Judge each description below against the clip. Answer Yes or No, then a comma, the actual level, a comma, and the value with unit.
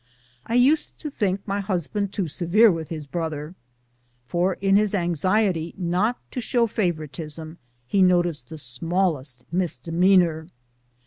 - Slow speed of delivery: Yes, slow, 130 wpm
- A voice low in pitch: No, medium, 175 Hz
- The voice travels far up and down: No, average, 3.8 semitones